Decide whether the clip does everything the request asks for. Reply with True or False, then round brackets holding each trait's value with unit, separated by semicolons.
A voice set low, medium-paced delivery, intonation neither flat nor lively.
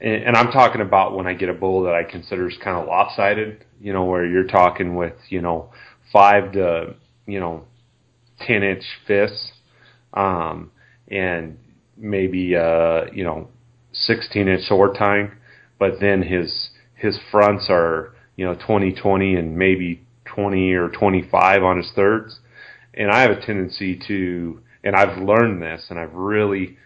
True (100 Hz; 160 wpm; 3.1 semitones)